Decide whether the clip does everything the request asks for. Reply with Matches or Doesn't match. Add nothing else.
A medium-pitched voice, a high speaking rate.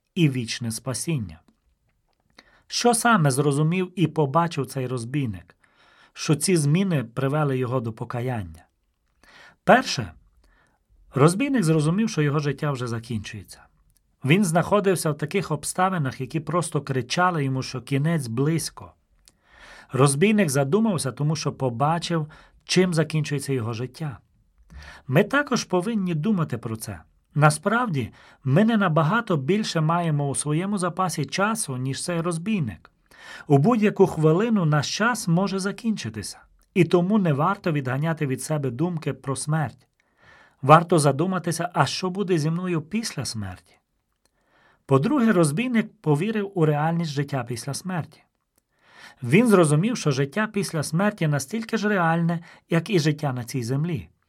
Doesn't match